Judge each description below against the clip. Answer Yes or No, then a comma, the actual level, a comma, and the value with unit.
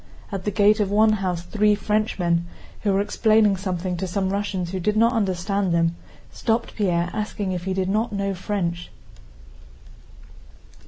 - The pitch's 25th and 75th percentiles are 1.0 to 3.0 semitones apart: Yes, average, 2.7 semitones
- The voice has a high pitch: Yes, high, 195 Hz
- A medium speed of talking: Yes, average, 160 wpm